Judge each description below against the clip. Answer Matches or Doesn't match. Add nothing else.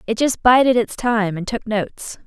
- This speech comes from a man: Doesn't match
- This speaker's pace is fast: Matches